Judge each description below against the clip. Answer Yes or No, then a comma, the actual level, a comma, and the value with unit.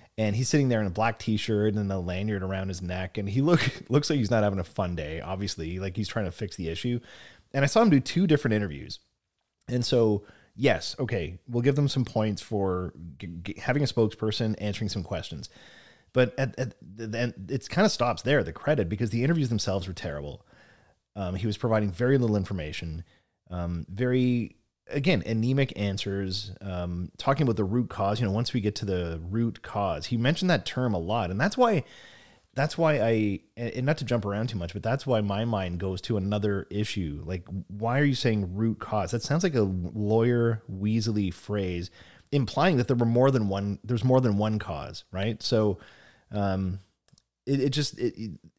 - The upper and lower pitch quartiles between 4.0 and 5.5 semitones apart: Yes, average, 4.3 semitones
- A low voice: Yes, low, 110 Hz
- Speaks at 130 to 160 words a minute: No, fast, 205 wpm